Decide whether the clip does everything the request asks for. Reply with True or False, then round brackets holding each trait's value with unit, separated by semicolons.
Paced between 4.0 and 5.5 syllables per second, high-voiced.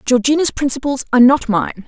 False (5.9 syllables/s; 255 Hz)